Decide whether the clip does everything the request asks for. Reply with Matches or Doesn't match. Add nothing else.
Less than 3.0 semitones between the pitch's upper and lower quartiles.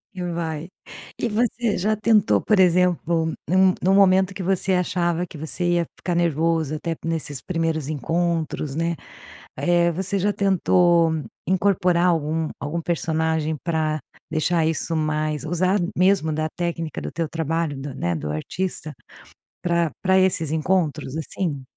Matches